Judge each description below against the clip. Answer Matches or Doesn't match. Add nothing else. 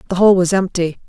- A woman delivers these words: Matches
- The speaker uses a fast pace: Matches